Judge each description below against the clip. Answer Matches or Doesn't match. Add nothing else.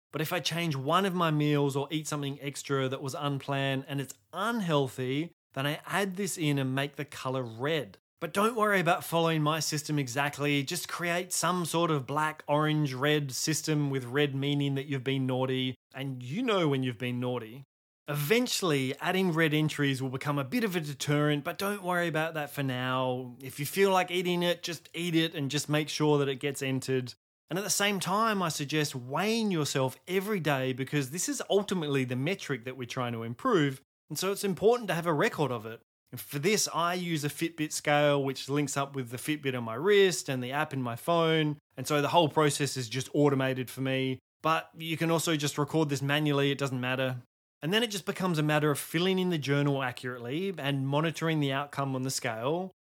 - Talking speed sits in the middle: Doesn't match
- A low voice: Doesn't match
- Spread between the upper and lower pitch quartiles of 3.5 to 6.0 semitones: Matches